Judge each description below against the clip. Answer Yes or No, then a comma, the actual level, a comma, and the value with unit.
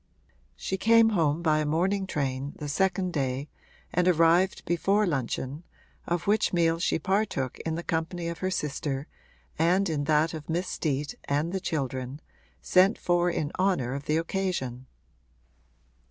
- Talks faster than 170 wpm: No, average, 155 wpm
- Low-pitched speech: No, medium, 165 Hz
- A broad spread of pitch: No, average, 4.1 semitones